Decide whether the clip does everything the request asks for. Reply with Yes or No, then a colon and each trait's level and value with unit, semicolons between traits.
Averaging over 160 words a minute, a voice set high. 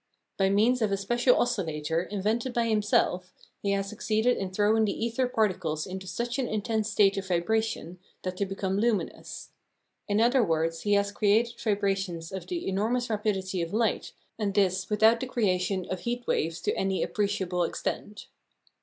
Yes: average, 170 wpm; high, 205 Hz